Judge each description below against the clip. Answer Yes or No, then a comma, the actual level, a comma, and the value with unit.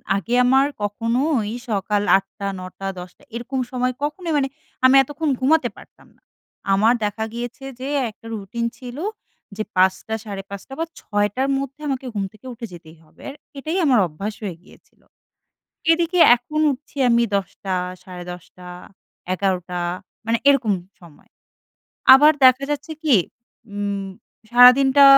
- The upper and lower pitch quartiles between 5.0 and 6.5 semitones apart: Yes, wide, 5.4 semitones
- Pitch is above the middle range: Yes, high, 235 Hz